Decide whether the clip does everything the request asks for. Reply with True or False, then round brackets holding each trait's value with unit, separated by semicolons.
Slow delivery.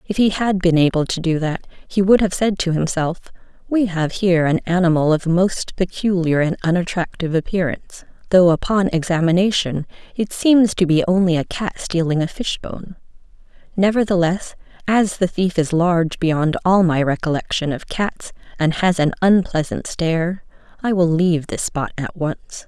False (165 wpm)